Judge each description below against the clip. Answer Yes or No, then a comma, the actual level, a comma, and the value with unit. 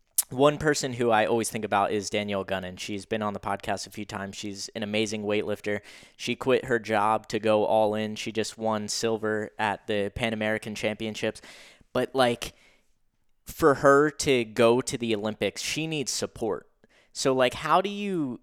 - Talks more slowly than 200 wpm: Yes, average, 180 wpm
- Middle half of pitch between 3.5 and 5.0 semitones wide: No, average, 2.7 semitones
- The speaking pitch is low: Yes, low, 110 Hz